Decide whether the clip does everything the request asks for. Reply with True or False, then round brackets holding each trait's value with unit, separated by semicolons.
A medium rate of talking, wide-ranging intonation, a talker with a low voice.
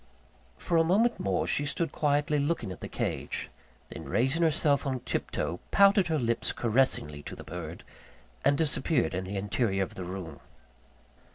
True (170 wpm; 8.8 semitones; 130 Hz)